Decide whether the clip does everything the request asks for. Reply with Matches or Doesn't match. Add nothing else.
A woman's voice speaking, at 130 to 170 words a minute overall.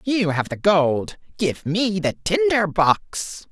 Doesn't match